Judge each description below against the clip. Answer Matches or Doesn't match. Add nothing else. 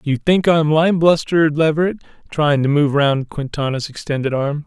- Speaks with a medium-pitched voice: Matches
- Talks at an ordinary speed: Matches